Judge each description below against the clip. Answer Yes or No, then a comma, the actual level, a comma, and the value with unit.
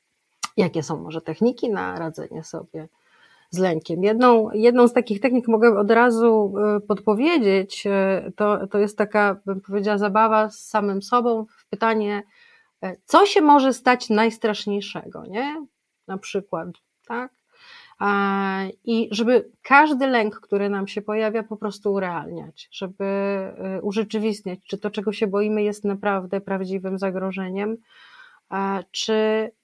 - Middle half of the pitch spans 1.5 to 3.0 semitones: Yes, average, 2.7 semitones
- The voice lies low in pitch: No, high, 210 Hz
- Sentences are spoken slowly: No, average, 125 wpm